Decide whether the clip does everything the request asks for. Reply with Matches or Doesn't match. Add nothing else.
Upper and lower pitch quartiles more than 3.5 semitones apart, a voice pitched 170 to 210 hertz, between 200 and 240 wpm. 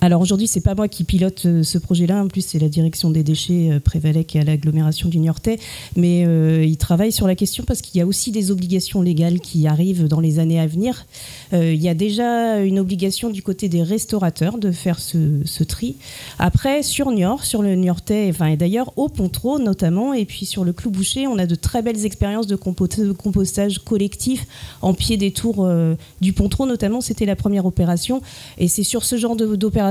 Matches